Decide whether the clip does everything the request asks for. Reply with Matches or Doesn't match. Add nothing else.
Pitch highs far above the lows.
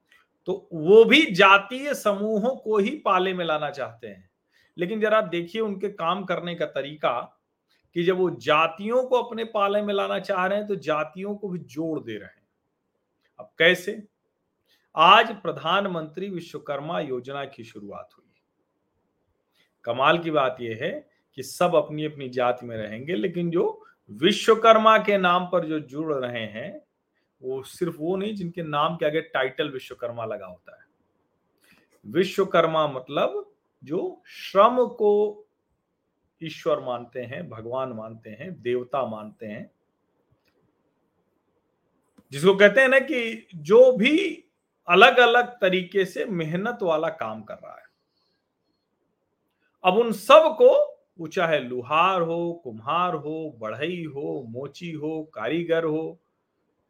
Matches